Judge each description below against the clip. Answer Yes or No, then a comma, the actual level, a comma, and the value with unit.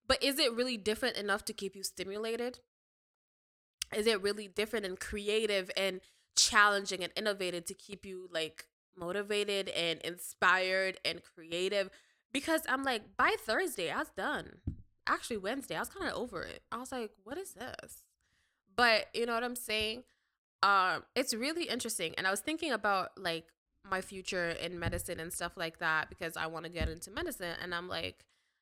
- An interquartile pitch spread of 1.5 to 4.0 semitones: No, average, 4.5 semitones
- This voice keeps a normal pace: Yes, average, 180 wpm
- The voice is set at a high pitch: Yes, high, 200 Hz